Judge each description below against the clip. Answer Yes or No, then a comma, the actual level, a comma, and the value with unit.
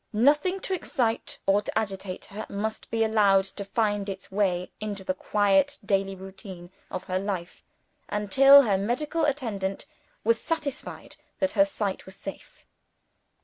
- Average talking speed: Yes, average, 145 wpm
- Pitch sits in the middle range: No, high, 205 Hz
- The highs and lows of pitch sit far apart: No, average, 3.8 semitones